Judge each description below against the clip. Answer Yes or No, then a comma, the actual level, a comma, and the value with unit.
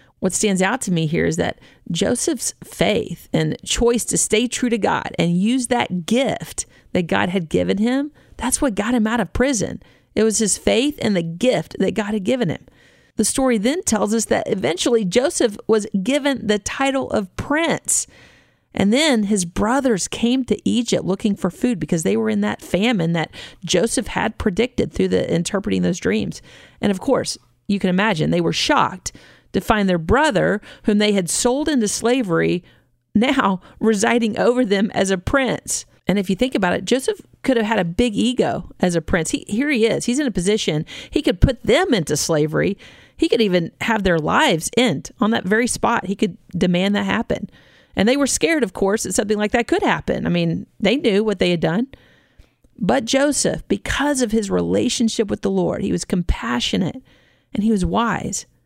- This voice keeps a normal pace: Yes, average, 195 wpm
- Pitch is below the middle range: No, high, 220 Hz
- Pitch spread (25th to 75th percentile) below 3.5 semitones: No, average, 4.6 semitones